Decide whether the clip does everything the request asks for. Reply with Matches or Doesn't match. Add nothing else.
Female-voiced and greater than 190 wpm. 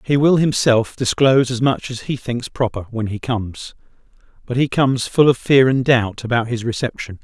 Doesn't match